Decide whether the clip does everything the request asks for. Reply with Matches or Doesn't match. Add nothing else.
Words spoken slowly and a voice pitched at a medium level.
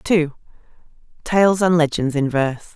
Matches